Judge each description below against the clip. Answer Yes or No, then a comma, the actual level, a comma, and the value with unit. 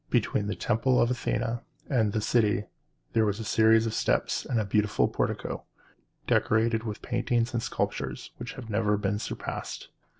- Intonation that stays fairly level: Yes, narrow, 2.0 semitones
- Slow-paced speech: No, average, 160 wpm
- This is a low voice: Yes, low, 110 Hz